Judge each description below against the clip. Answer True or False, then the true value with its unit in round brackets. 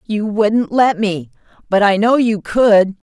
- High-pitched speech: True (210 Hz)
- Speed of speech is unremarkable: True (175 wpm)